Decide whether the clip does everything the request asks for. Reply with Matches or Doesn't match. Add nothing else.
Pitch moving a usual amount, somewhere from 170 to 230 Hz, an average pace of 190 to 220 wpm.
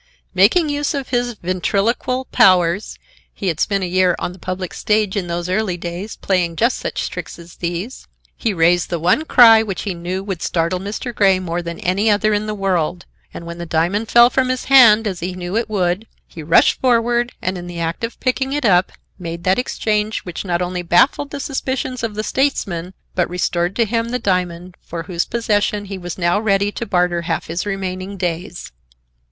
Matches